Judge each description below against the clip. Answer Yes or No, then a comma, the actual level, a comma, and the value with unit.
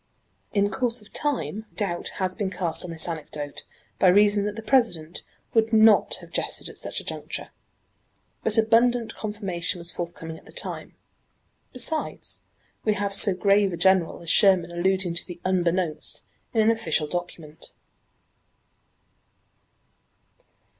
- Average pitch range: Yes, average, 4.1 semitones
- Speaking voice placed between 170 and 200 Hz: Yes, high, 190 Hz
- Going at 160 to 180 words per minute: No, average, 140 wpm